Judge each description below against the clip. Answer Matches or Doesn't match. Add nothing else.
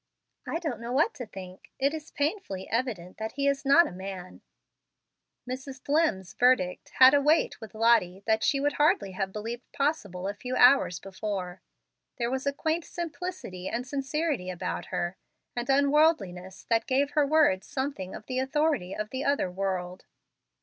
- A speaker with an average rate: Matches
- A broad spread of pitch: Matches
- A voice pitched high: Matches